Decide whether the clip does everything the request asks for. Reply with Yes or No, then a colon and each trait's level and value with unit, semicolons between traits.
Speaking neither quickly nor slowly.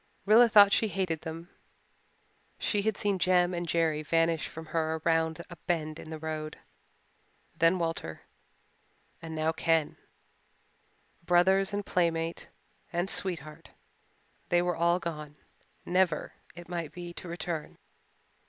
No: slow, 130 wpm